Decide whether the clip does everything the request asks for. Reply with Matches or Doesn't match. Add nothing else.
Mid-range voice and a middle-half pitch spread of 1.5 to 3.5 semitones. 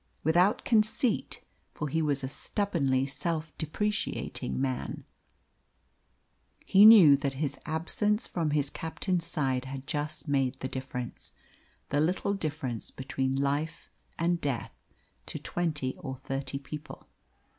Doesn't match